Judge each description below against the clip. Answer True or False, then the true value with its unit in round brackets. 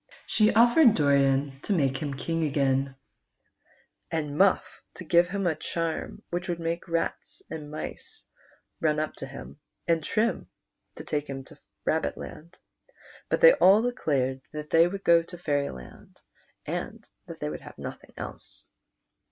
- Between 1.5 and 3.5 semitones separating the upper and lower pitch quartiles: False (4.0 semitones)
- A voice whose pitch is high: False (160 Hz)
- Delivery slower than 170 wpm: True (155 wpm)